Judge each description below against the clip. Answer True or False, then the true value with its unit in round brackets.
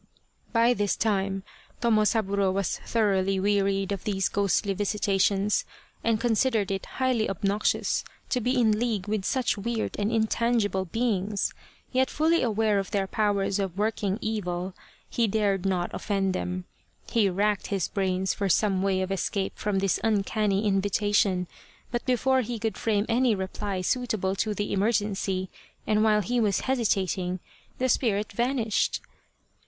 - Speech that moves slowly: False (150 wpm)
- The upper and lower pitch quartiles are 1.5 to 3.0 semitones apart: True (2.4 semitones)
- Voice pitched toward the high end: True (205 Hz)